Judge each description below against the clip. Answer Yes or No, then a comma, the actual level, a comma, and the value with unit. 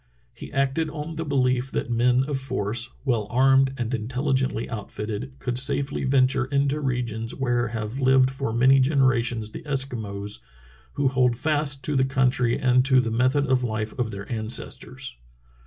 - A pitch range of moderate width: No, narrow, 2.3 semitones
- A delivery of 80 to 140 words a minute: No, average, 160 wpm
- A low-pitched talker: Yes, low, 130 Hz